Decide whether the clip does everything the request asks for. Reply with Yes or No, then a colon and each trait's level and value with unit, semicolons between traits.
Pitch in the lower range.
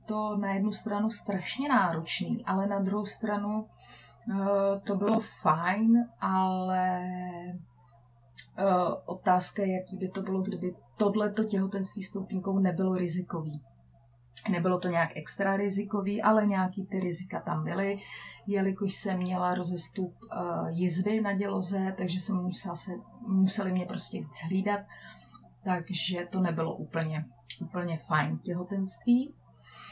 No: high, 190 Hz